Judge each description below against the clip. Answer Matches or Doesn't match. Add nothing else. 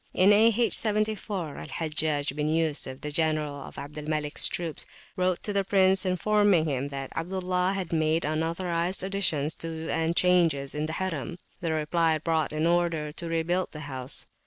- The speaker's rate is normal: Matches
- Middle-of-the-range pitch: Matches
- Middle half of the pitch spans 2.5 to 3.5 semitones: Matches